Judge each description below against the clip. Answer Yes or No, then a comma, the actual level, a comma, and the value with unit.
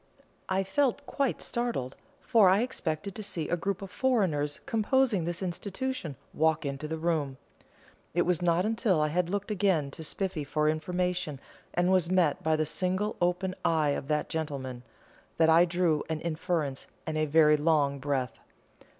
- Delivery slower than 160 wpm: No, average, 165 wpm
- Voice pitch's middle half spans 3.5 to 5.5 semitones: Yes, average, 3.9 semitones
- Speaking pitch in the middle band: Yes, medium, 170 Hz